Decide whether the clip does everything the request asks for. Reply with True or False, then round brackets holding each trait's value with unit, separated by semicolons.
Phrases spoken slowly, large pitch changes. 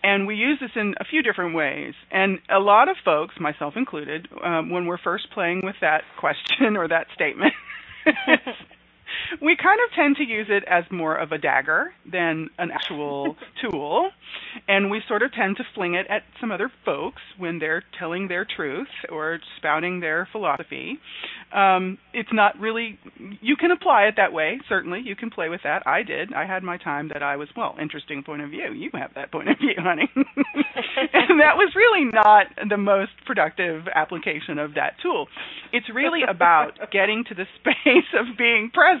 False (190 wpm; 7.8 semitones)